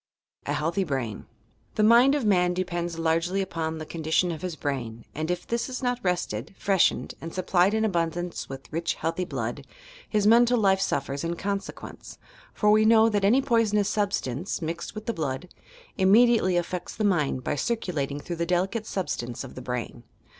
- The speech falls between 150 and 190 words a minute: Yes, average, 180 wpm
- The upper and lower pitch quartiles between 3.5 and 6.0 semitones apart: Yes, average, 4.7 semitones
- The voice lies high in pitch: No, medium, 180 Hz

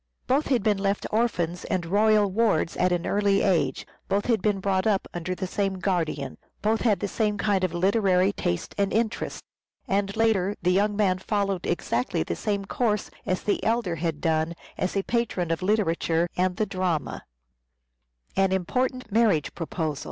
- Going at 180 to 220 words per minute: No, average, 160 wpm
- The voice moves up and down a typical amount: Yes, average, 3.0 semitones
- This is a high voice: Yes, high, 195 Hz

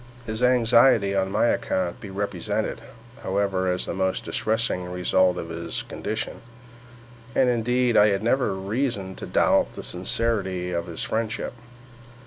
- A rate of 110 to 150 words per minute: Yes, average, 140 wpm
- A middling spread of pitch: Yes, average, 3.8 semitones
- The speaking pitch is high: No, low, 100 Hz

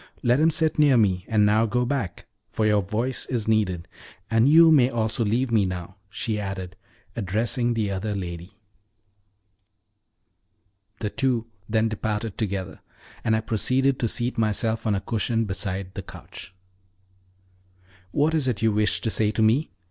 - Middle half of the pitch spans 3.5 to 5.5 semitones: No, average, 3.0 semitones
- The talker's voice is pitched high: No, low, 110 Hz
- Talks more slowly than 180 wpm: Yes, average, 160 wpm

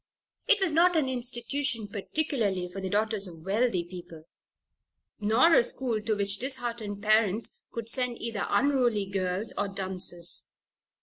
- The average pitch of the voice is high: Yes, high, 215 Hz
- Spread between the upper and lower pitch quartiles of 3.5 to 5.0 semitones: Yes, average, 4.3 semitones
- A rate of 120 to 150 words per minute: Yes, average, 140 wpm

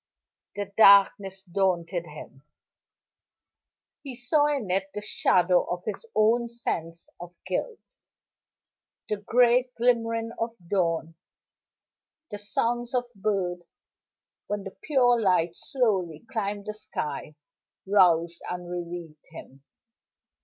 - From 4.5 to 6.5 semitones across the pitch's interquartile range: Yes, average, 4.8 semitones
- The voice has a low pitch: No, high, 200 Hz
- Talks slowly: Yes, slow, 110 wpm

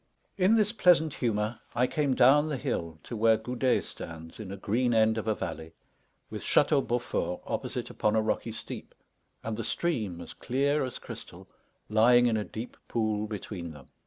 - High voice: No, low, 115 Hz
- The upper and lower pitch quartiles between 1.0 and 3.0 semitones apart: No, average, 3.8 semitones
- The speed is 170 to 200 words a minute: Yes, average, 180 wpm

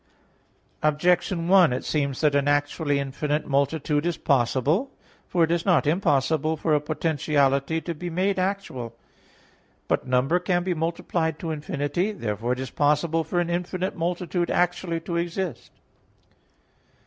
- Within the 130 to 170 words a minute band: Yes, average, 145 wpm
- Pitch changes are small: No, average, 3.5 semitones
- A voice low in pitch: No, medium, 160 Hz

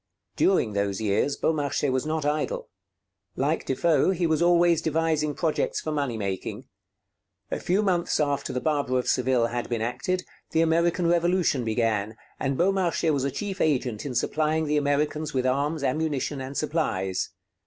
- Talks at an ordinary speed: Yes, average, 160 wpm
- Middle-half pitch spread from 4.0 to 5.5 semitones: Yes, average, 4.3 semitones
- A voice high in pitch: No, medium, 150 Hz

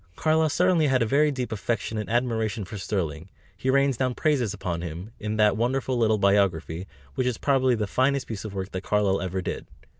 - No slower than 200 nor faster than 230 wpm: Yes, fast, 205 wpm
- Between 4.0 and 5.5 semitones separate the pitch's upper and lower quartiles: Yes, average, 4.8 semitones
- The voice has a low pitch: Yes, low, 110 Hz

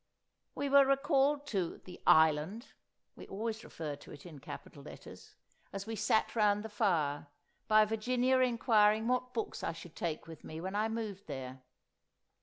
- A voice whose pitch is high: Yes, high, 210 Hz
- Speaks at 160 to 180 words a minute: Yes, average, 165 wpm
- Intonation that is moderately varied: No, wide, 6.0 semitones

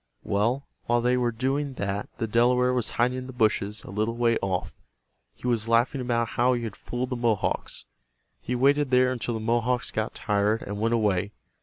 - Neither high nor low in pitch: No, low, 120 Hz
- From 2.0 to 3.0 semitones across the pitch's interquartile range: Yes, narrow, 2.5 semitones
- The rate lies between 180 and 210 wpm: Yes, average, 195 wpm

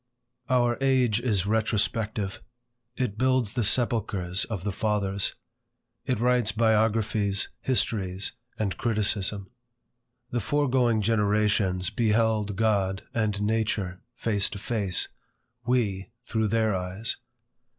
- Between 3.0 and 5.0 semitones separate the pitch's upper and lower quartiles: No, narrow, 2.6 semitones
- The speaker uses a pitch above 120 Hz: No, low, 110 Hz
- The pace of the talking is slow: Yes, slow, 105 wpm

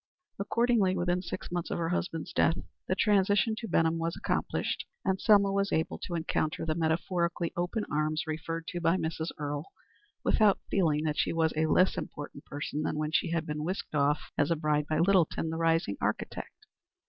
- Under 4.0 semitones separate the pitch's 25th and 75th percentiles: Yes, average, 3.0 semitones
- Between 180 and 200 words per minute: Yes, average, 185 wpm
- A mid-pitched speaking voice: Yes, medium, 165 Hz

